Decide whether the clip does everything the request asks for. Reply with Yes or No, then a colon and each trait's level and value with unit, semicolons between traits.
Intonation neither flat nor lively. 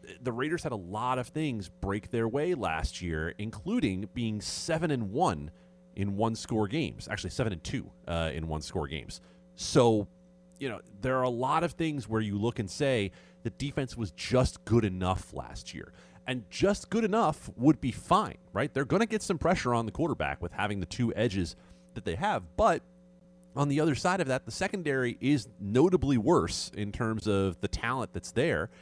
No: wide, 7.3 semitones